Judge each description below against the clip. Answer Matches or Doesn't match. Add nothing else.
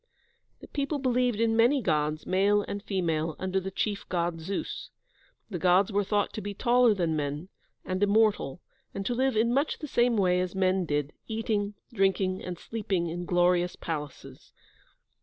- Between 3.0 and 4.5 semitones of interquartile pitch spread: Matches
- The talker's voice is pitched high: Matches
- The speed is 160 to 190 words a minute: Matches